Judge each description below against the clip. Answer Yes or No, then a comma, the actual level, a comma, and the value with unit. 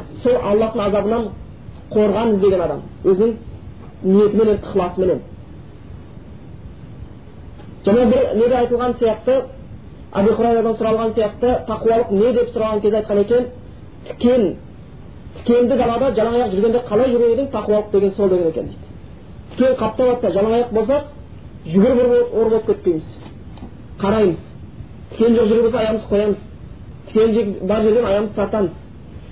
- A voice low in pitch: No, high, 225 Hz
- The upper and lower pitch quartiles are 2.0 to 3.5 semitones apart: Yes, average, 2.8 semitones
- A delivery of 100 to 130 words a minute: Yes, average, 120 wpm